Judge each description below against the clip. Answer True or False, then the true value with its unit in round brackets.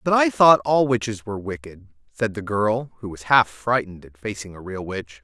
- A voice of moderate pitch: False (110 Hz)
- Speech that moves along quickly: True (220 wpm)